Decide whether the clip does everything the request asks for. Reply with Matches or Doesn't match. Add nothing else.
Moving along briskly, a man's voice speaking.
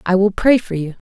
Doesn't match